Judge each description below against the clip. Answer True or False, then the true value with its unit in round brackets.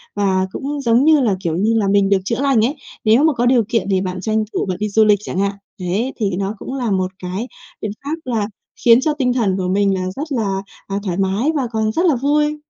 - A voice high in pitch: True (215 Hz)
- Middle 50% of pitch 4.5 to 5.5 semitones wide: True (4.9 semitones)